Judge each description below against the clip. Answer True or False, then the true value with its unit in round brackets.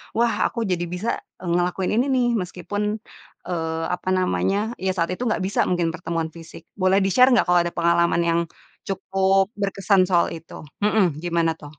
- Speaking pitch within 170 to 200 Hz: True (185 Hz)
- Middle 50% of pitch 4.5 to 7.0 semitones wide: False (2.6 semitones)